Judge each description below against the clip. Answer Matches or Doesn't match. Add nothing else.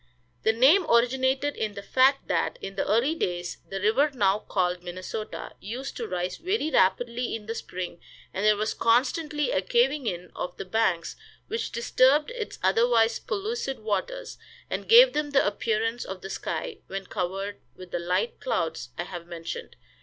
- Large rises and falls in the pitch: Matches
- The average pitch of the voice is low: Doesn't match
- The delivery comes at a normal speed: Matches